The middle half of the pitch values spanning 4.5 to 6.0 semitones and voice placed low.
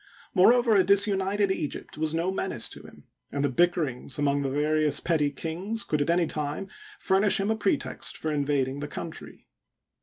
No: average, 4.9 semitones; medium, 160 Hz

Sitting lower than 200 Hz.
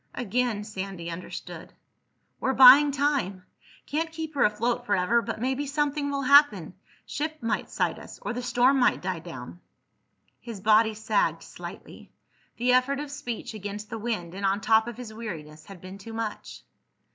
No: high, 230 Hz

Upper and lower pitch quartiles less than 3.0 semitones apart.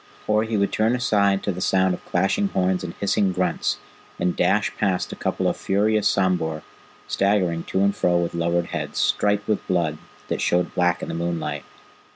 Yes: narrow, 2.6 semitones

